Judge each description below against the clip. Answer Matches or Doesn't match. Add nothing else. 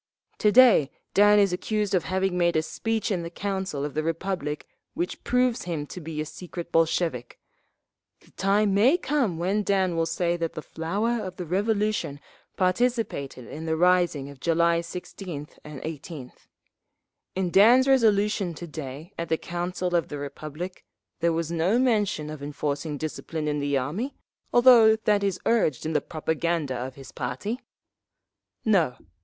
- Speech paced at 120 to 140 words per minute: Doesn't match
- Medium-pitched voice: Matches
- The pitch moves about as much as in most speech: Matches